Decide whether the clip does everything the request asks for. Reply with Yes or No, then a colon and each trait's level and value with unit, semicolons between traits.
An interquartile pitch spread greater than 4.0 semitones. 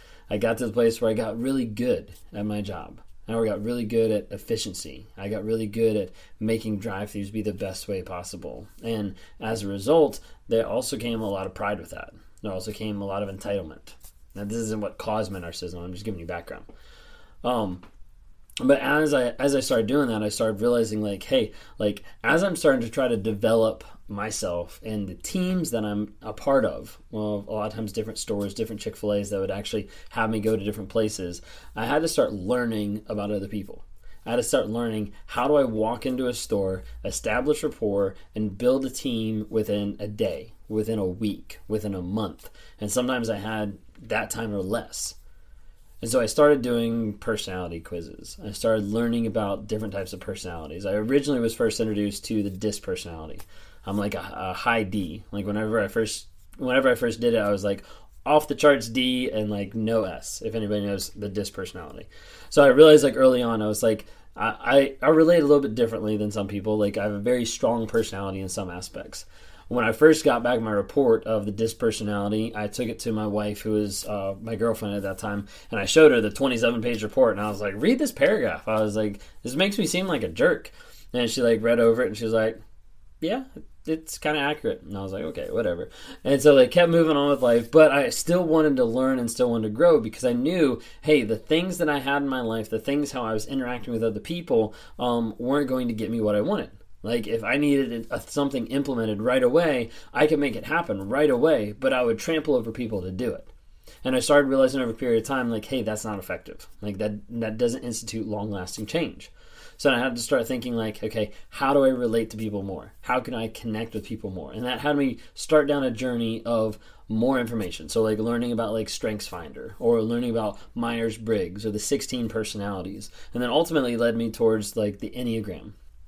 No: average, 3.2 semitones